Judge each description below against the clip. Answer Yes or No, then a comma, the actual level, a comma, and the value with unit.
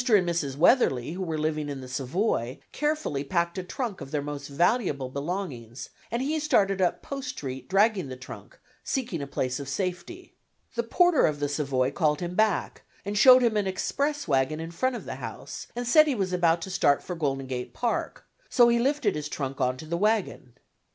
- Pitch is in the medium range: Yes, medium, 175 Hz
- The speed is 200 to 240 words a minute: Yes, fast, 205 wpm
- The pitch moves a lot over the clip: Yes, wide, 8.3 semitones